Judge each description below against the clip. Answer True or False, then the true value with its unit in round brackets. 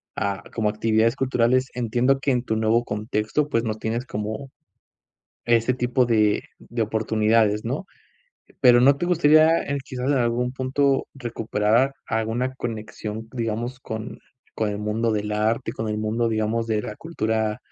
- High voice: False (115 Hz)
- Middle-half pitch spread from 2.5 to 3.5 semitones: True (2.8 semitones)